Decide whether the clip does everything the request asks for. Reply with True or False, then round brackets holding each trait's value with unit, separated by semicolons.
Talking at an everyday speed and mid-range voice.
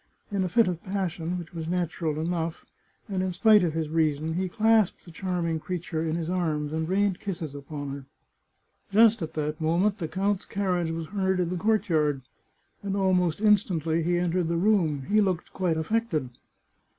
True (180 wpm; 175 Hz)